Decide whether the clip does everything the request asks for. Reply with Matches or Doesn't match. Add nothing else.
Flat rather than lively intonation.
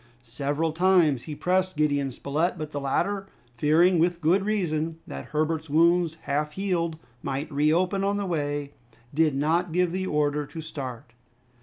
Doesn't match